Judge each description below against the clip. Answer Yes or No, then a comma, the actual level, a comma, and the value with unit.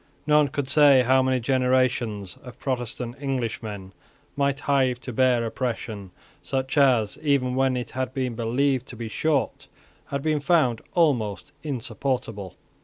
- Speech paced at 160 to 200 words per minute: No, average, 140 wpm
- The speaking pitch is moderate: No, low, 130 Hz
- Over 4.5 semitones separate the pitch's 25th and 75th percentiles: No, average, 2.9 semitones